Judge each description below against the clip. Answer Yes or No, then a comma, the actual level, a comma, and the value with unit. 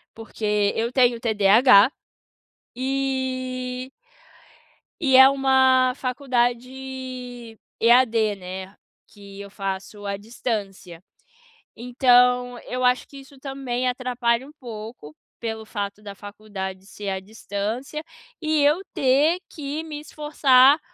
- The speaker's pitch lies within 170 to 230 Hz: No, high, 245 Hz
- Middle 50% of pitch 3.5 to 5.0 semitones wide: Yes, average, 4.0 semitones